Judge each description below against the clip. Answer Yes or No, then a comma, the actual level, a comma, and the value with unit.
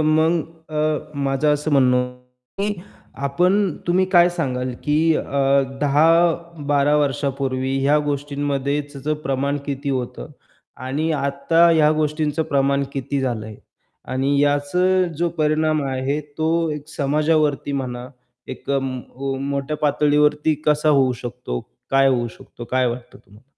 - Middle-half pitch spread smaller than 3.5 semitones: Yes, narrow, 2.4 semitones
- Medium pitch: Yes, medium, 145 Hz